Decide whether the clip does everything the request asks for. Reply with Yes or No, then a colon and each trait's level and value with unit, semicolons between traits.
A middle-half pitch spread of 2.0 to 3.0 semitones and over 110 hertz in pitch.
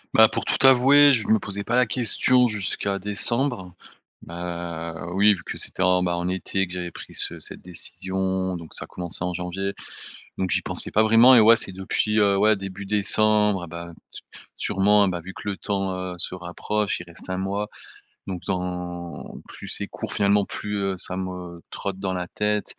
No: average, 2.7 semitones; very low, 95 Hz